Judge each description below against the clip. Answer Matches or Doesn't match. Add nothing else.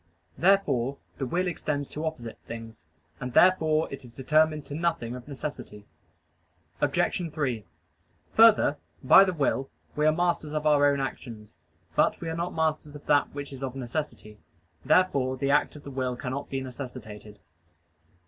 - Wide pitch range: Doesn't match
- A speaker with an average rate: Matches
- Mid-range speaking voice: Matches